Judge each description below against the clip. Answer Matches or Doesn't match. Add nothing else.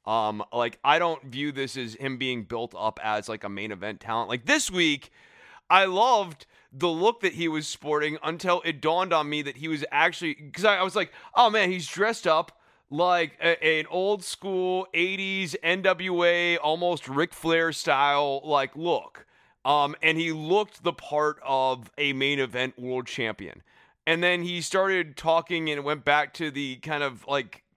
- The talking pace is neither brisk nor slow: Matches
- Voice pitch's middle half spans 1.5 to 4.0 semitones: Doesn't match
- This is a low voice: Doesn't match